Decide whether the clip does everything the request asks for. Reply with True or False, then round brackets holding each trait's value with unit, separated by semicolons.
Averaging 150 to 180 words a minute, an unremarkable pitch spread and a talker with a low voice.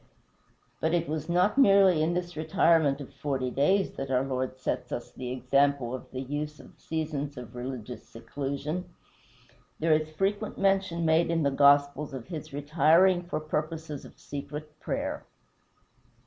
False (155 wpm; 3.4 semitones; 150 Hz)